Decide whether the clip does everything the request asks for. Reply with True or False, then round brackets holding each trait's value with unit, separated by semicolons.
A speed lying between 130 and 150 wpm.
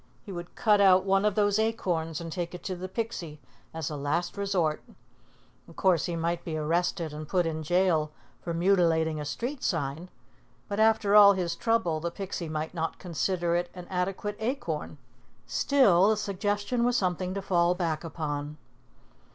False (175 wpm)